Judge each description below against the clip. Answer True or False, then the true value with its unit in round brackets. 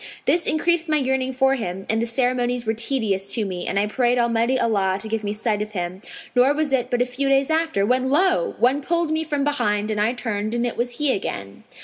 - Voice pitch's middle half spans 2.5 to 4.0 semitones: False (4.4 semitones)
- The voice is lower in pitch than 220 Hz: False (245 Hz)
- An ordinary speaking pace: False (240 wpm)